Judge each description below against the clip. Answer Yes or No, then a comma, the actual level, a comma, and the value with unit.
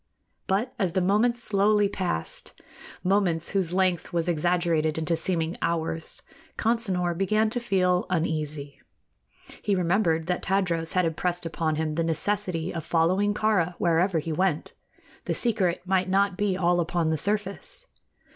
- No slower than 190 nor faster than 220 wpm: No, average, 145 wpm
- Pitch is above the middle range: No, medium, 180 Hz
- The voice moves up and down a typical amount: Yes, average, 3.2 semitones